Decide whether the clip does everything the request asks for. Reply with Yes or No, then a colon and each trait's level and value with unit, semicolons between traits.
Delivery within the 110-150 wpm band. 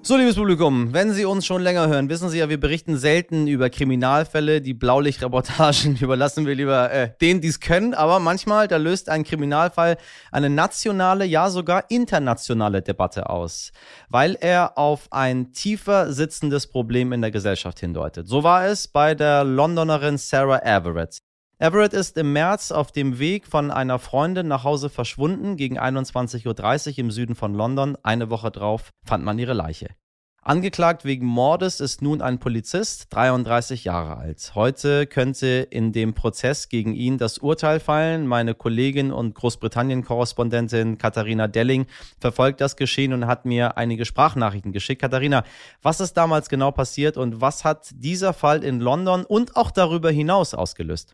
No: average, 165 wpm